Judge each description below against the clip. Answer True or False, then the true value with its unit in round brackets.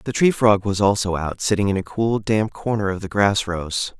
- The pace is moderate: False (240 wpm)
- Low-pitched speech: True (100 Hz)